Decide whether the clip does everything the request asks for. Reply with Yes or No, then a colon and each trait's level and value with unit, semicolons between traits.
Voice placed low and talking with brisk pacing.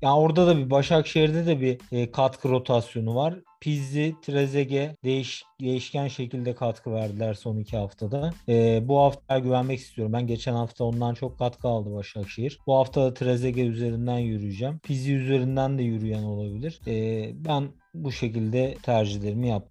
Yes: low, 130 Hz; fast, 155 wpm